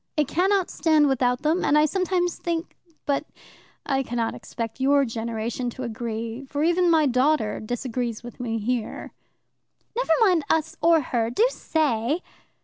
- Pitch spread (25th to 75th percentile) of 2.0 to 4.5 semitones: No, wide, 5.5 semitones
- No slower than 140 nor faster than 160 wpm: Yes, average, 150 wpm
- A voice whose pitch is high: Yes, very high, 270 Hz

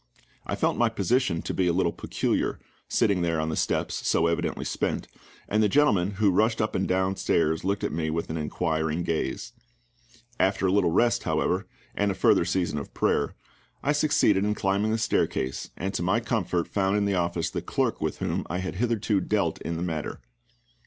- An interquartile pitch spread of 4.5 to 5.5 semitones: No, average, 3.8 semitones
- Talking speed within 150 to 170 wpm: No, average, 195 wpm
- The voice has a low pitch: Yes, very low, 95 Hz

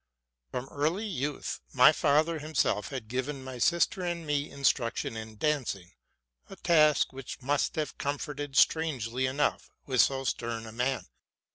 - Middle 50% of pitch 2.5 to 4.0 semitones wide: Yes, average, 3.4 semitones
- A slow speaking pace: No, average, 150 wpm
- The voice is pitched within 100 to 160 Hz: Yes, medium, 140 Hz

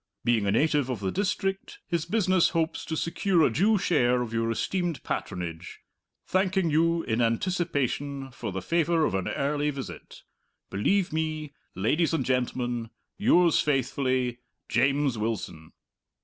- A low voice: No, medium, 145 Hz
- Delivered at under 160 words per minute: Yes, average, 140 wpm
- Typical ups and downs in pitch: No, wide, 6.1 semitones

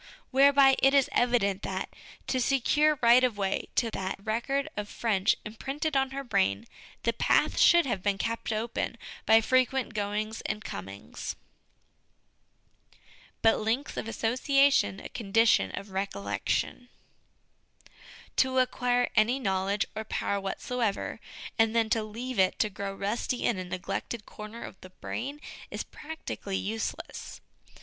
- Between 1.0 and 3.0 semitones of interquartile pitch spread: No, average, 4.3 semitones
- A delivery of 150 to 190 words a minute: No, average, 140 wpm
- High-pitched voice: Yes, high, 225 Hz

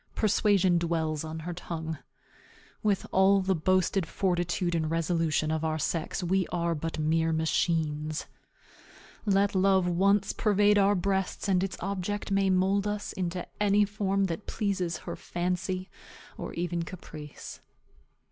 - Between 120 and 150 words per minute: Yes, average, 140 wpm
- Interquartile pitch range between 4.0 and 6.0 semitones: No, average, 3.1 semitones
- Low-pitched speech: No, medium, 180 Hz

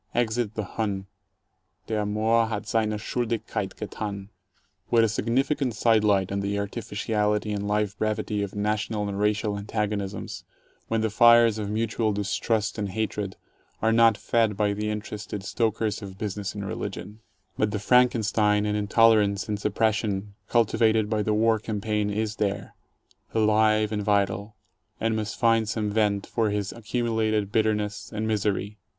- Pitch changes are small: Yes, narrow, 1.4 semitones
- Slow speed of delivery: No, average, 155 wpm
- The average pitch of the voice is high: No, low, 105 Hz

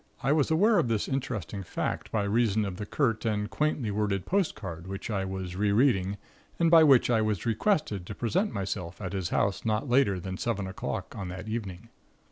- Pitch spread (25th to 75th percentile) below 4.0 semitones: No, average, 4.5 semitones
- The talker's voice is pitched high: No, low, 105 Hz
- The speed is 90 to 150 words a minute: No, average, 195 wpm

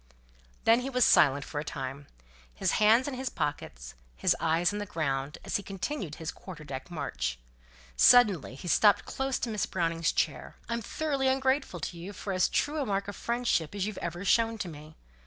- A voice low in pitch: No, high, 195 Hz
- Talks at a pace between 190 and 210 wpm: Yes, average, 195 wpm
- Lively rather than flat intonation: Yes, wide, 7.3 semitones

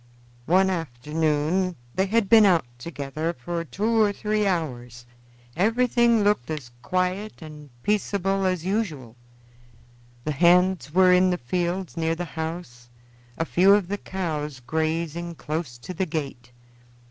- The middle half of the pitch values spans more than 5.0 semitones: No, average, 4.0 semitones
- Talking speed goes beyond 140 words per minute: No, slow, 135 wpm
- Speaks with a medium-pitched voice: Yes, medium, 170 Hz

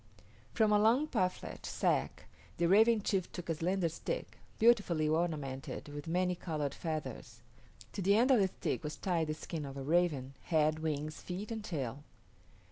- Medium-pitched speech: Yes, medium, 170 Hz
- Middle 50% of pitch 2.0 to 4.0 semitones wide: No, average, 4.4 semitones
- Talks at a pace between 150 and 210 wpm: Yes, average, 170 wpm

